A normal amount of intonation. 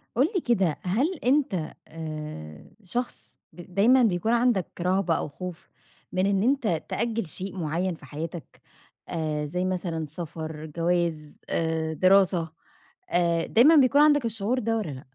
No: wide, 6.0 semitones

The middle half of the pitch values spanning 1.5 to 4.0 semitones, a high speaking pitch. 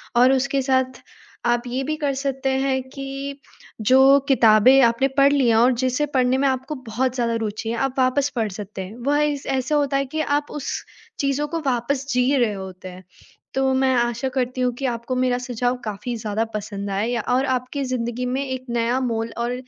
Yes: narrow, 2.5 semitones; very high, 255 Hz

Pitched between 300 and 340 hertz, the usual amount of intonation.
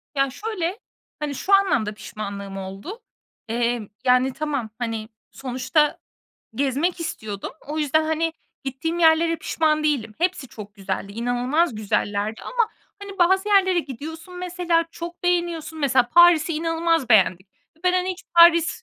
No: very high, 310 Hz; wide, 6.2 semitones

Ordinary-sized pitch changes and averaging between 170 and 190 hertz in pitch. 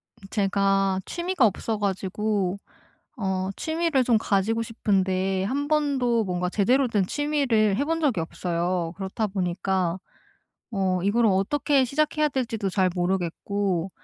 No: average, 5.0 semitones; high, 200 Hz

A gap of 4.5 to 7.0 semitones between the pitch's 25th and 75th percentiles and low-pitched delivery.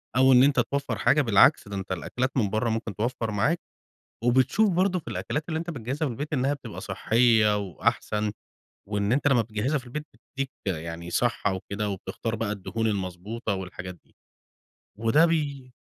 Yes: average, 5.2 semitones; low, 115 Hz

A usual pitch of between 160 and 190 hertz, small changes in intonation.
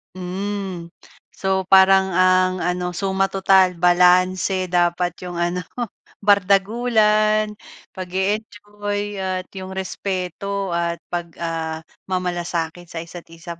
Yes: medium, 185 Hz; narrow, 1.9 semitones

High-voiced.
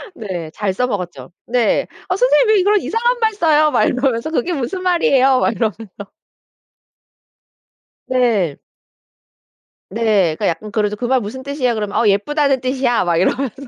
Yes: very high, 250 Hz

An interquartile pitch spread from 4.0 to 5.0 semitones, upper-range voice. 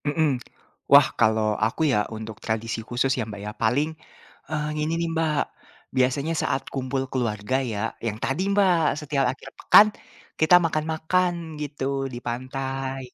No: average, 4.6 semitones; low, 135 Hz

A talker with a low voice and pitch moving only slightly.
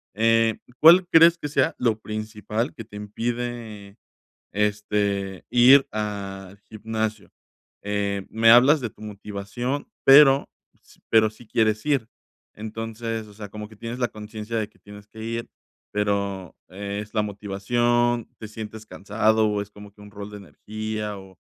Yes: low, 110 Hz; narrow, 2.1 semitones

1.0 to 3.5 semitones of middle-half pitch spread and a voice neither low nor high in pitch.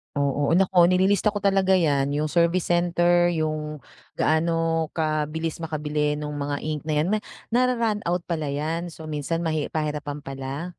Yes: narrow, 2.6 semitones; medium, 160 Hz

